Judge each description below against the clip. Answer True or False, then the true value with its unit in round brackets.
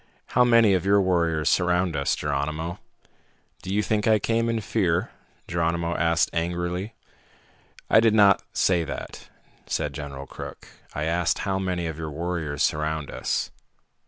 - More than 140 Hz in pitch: False (85 Hz)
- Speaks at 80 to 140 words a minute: False (150 wpm)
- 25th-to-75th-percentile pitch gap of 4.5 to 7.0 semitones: False (3.5 semitones)